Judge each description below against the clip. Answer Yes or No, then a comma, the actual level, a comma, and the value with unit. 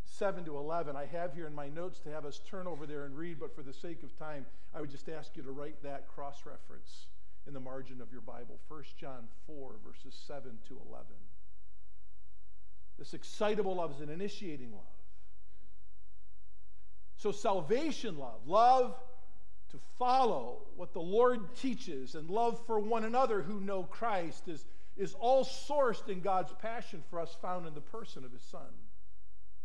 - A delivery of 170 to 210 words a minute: Yes, average, 175 wpm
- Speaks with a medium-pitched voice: Yes, medium, 150 Hz